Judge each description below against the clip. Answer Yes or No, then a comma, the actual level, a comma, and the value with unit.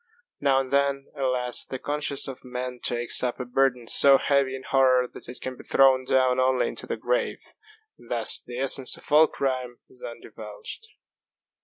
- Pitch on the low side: Yes, low, 130 Hz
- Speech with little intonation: Yes, narrow, 1.7 semitones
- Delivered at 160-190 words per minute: Yes, average, 180 wpm